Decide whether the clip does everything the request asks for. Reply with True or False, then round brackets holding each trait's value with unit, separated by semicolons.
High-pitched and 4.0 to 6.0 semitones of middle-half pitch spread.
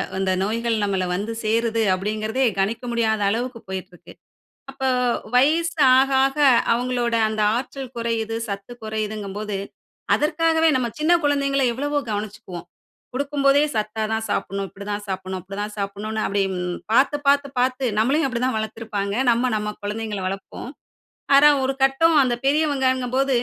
True (230 Hz; 4.5 semitones)